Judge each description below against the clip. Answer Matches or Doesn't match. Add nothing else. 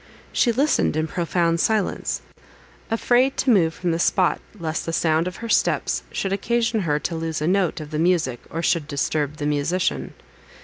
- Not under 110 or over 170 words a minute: Doesn't match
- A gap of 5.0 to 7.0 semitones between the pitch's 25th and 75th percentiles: Doesn't match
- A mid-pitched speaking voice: Matches